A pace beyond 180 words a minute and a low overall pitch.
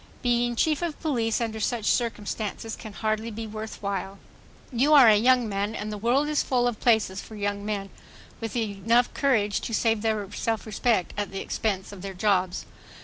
No: average, 190 wpm; high, 220 Hz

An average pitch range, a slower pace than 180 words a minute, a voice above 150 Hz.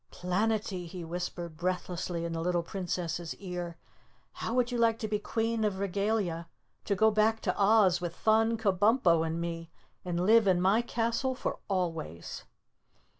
Yes: average, 4.2 semitones; average, 160 wpm; medium, 185 Hz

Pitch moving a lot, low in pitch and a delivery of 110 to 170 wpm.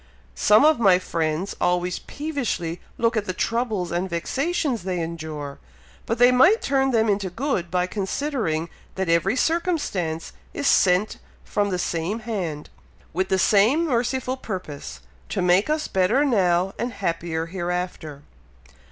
No: wide, 6.0 semitones; high, 190 Hz; average, 145 wpm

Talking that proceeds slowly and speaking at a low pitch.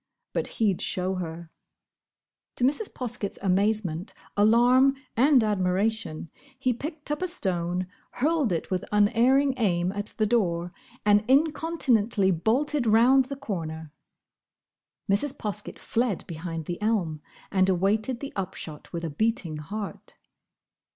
No: slow, 125 wpm; high, 210 Hz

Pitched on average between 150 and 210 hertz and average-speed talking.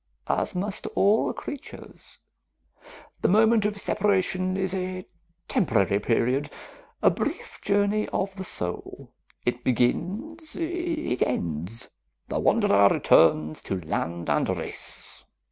No: medium, 185 Hz; slow, 110 wpm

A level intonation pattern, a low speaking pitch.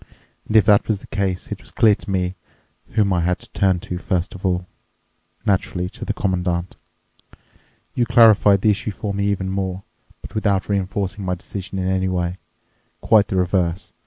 Yes: narrow, 1.9 semitones; very low, 95 Hz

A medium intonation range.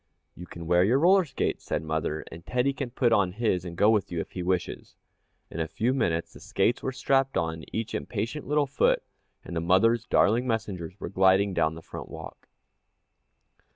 No: wide, 6.3 semitones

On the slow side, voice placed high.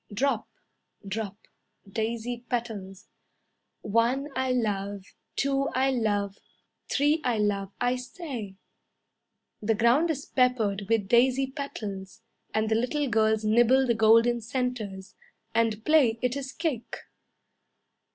Yes: slow, 115 wpm; high, 230 Hz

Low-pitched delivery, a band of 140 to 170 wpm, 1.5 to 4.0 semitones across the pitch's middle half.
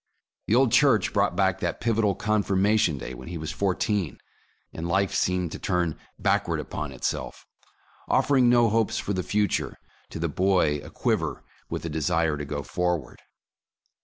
No: very low, 90 Hz; average, 160 wpm; average, 4.6 semitones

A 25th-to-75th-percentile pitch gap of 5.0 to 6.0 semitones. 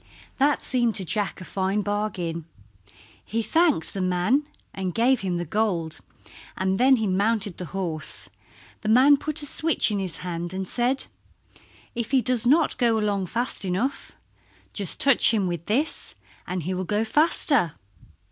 Yes: wide, 5.4 semitones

